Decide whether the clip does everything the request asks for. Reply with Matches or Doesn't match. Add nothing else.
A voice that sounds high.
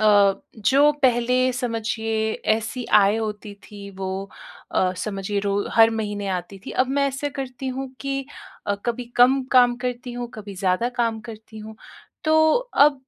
Matches